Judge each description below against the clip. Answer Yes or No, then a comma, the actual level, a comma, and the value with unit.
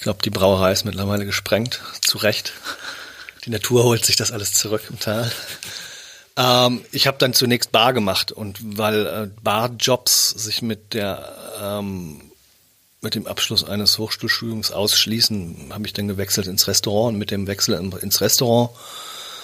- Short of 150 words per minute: No, average, 155 wpm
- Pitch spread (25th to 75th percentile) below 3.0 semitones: No, average, 3.3 semitones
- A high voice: No, low, 110 Hz